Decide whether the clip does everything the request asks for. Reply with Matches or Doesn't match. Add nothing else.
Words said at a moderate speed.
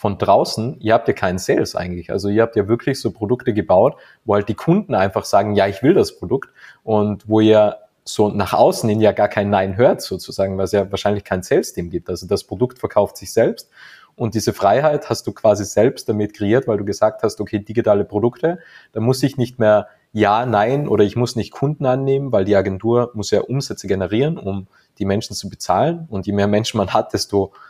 Doesn't match